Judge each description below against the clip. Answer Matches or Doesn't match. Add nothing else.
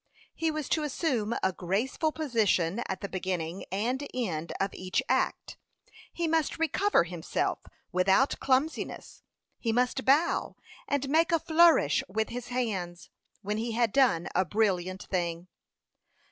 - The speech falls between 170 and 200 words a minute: Doesn't match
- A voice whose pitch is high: Matches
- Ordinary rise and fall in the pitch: Doesn't match